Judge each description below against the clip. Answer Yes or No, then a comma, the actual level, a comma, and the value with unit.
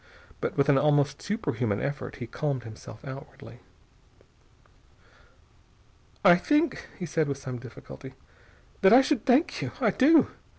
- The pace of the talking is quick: No, slow, 135 wpm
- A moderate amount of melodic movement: No, wide, 7.7 semitones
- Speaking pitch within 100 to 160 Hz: Yes, medium, 140 Hz